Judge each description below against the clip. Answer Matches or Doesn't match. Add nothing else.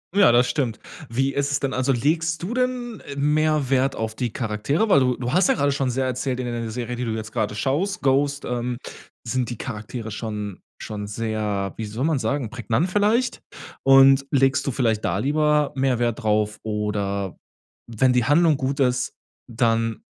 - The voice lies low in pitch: Matches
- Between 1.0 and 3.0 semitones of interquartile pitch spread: Doesn't match